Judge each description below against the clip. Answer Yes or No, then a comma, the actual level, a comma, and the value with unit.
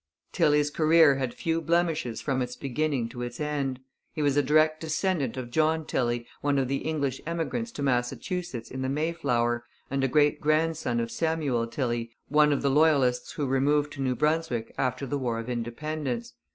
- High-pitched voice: No, medium, 140 Hz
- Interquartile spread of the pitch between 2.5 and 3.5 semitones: No, average, 3.9 semitones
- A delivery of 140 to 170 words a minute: No, average, 180 wpm